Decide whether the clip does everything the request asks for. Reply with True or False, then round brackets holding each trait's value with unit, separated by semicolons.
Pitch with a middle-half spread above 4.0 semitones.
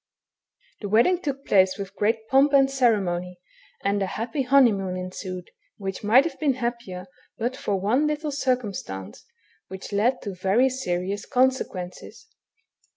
True (5.5 semitones)